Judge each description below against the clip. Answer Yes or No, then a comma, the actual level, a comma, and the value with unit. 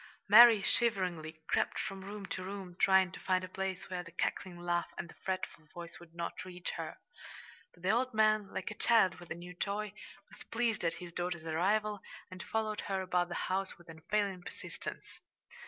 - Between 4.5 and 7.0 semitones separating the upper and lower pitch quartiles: No, average, 2.8 semitones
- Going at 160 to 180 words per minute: No, average, 190 wpm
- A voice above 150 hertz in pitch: Yes, medium, 185 Hz